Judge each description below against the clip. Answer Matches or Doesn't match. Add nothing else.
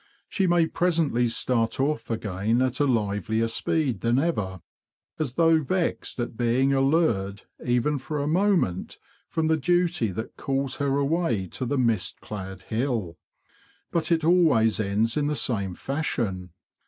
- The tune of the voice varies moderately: Doesn't match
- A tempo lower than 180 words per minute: Matches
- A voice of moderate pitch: Doesn't match